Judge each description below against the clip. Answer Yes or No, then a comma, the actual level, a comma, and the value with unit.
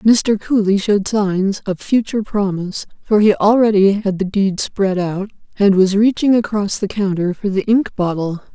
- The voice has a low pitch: No, high, 200 Hz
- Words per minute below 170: No, average, 175 wpm